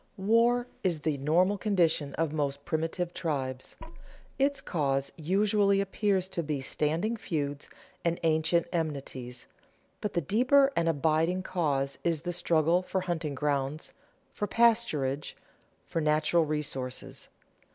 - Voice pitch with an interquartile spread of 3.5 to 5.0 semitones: Yes, average, 4.5 semitones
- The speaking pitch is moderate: Yes, medium, 165 Hz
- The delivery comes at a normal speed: No, slow, 130 wpm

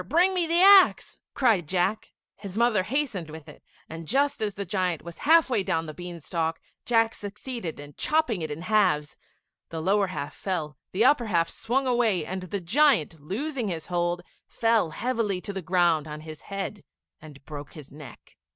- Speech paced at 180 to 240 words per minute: Yes, average, 185 wpm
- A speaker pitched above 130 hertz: Yes, high, 190 Hz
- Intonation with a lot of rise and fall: Yes, wide, 6.3 semitones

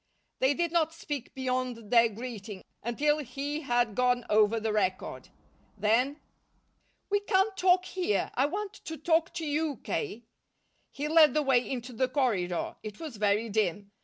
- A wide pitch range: Yes, wide, 5.7 semitones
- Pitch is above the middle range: Yes, very high, 255 Hz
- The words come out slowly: No, average, 160 wpm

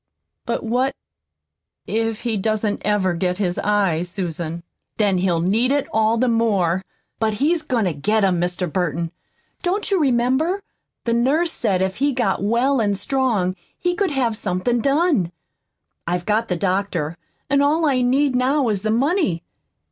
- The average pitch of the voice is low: No, high, 220 Hz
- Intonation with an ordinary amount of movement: No, wide, 6.1 semitones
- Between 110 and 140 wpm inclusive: No, average, 165 wpm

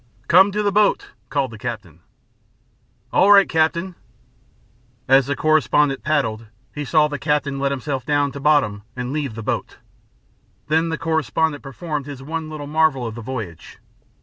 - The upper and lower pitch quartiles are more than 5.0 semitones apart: No, average, 3.3 semitones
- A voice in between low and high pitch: Yes, medium, 145 Hz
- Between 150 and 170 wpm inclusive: Yes, average, 160 wpm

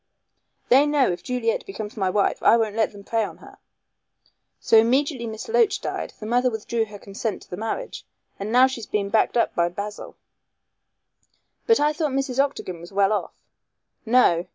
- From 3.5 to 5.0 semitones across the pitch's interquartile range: Yes, average, 4.2 semitones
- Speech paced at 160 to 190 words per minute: Yes, average, 185 wpm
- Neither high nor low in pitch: No, high, 225 Hz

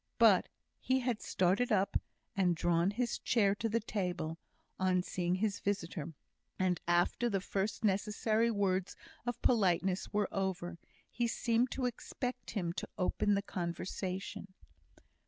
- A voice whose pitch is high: Yes, high, 195 Hz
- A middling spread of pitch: Yes, average, 3.5 semitones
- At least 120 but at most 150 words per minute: Yes, slow, 135 wpm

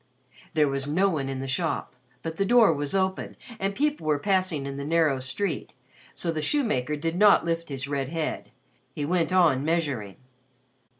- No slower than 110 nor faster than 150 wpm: No, average, 180 wpm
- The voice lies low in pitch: No, medium, 160 Hz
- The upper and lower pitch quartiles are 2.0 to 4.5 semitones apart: No, average, 4.9 semitones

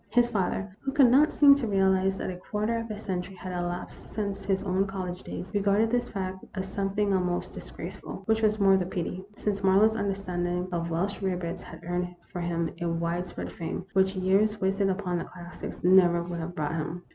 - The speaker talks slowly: No, fast, 205 wpm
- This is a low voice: No, high, 190 Hz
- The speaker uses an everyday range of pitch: No, narrow, 2.3 semitones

